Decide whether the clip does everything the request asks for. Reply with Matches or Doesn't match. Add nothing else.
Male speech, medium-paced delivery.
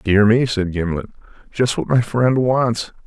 Matches